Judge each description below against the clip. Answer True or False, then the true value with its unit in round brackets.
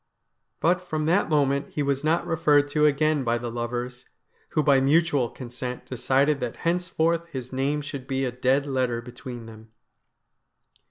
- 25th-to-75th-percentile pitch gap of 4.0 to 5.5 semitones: False (3.5 semitones)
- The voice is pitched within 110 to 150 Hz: True (140 Hz)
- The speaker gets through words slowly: False (160 wpm)